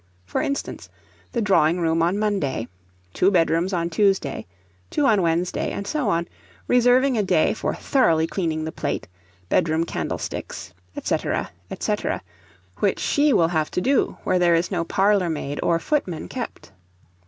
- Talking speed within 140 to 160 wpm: Yes, average, 155 wpm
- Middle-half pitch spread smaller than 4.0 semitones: No, average, 4.4 semitones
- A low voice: No, medium, 180 Hz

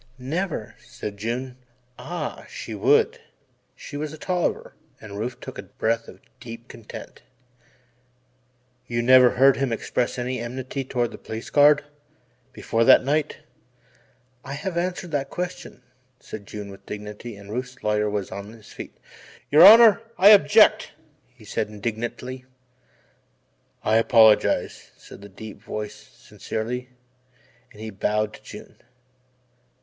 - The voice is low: Yes, low, 120 Hz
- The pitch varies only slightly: No, average, 5.1 semitones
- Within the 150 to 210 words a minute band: No, slow, 135 wpm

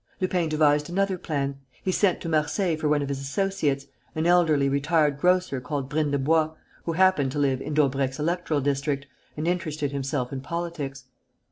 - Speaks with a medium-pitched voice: Yes, medium, 150 Hz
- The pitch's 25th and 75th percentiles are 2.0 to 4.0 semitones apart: Yes, average, 3.4 semitones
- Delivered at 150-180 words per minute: Yes, average, 165 wpm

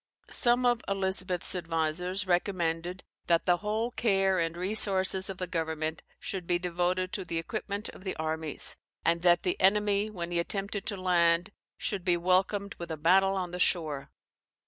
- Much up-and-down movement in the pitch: No, narrow, 2.5 semitones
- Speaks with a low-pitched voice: No, medium, 185 Hz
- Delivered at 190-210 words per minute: No, average, 170 wpm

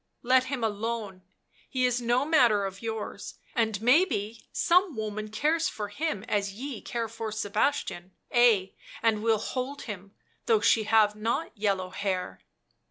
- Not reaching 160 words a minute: Yes, average, 150 wpm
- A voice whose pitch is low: No, high, 220 Hz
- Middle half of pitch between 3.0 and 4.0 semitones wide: Yes, average, 3.5 semitones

